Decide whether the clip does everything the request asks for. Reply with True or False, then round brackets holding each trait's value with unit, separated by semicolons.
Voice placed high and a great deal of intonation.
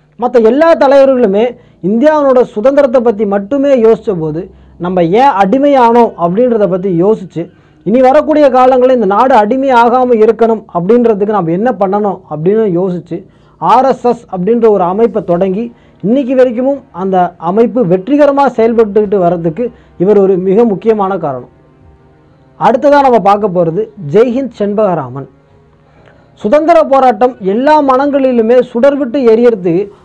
False (225 Hz; 5.0 semitones)